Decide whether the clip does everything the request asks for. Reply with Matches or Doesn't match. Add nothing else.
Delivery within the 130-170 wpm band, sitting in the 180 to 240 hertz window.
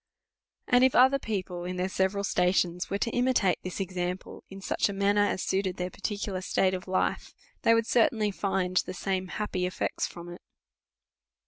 Doesn't match